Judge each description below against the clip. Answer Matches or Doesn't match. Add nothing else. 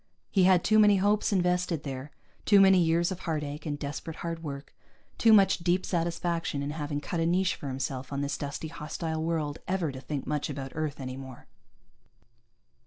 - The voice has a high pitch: Doesn't match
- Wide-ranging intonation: Doesn't match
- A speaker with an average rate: Matches